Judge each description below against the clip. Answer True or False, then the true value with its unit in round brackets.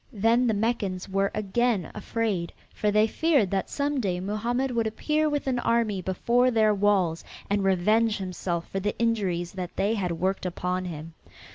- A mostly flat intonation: False (3.9 semitones)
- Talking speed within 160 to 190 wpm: True (170 wpm)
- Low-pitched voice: False (205 Hz)